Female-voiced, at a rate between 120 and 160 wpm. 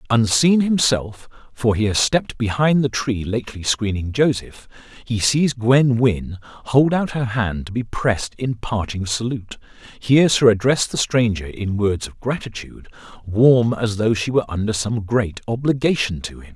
No: male; average, 155 wpm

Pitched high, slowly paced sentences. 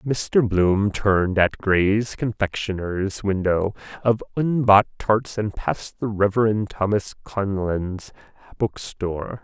No: low, 100 Hz; slow, 110 wpm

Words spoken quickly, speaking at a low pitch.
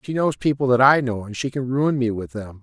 Yes: fast, 295 wpm; low, 130 Hz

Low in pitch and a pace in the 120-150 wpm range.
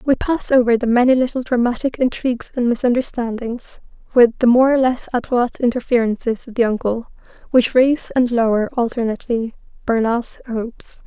No: high, 240 Hz; average, 145 wpm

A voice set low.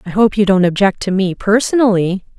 No: high, 200 Hz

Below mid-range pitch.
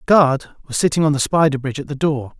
No: medium, 145 Hz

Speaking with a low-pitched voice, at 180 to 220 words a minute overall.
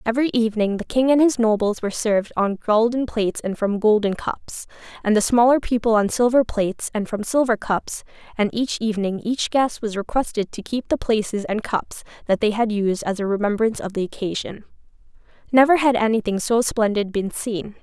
No: high, 220 Hz; average, 190 wpm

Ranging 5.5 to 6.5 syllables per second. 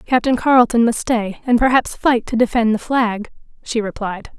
No: 4.9 syllables/s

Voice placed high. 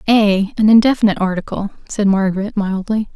Yes: high, 205 Hz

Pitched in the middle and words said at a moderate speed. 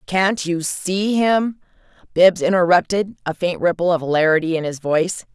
Yes: medium, 180 Hz; average, 155 wpm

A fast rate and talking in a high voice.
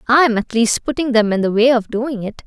Yes: fast, 290 wpm; high, 235 Hz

